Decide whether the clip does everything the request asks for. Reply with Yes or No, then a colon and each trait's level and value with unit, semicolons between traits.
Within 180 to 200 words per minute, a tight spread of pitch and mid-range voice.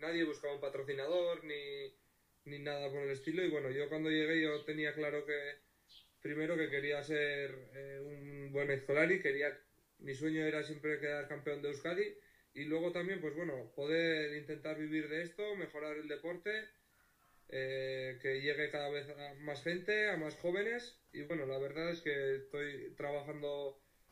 No: average, 170 wpm; narrow, 2.1 semitones; medium, 150 Hz